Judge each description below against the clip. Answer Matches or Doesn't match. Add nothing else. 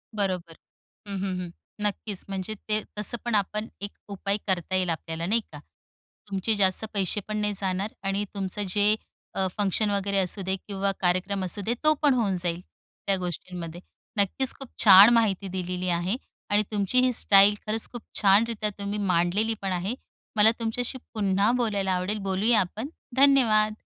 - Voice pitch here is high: Matches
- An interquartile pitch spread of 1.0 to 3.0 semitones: Matches